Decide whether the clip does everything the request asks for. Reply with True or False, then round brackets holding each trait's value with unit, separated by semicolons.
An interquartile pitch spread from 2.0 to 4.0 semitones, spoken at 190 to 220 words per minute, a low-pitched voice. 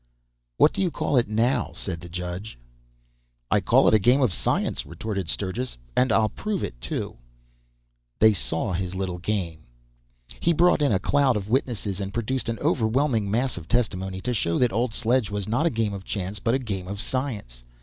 False (4.9 semitones; 195 wpm; 110 Hz)